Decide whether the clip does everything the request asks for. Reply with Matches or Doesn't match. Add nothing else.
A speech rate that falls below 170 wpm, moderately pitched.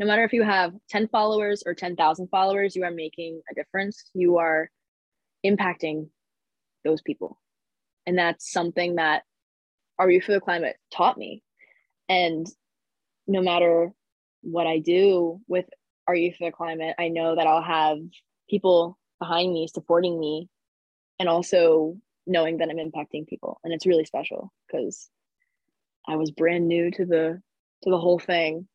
Matches